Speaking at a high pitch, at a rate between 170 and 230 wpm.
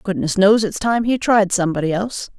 Yes: high, 200 Hz; average, 200 wpm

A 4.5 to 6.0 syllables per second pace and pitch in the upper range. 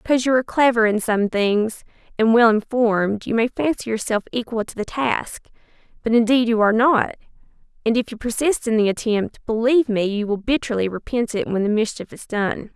Yes: 5.5 syllables/s; high, 230 Hz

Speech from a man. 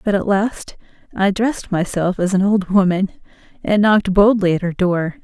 No: female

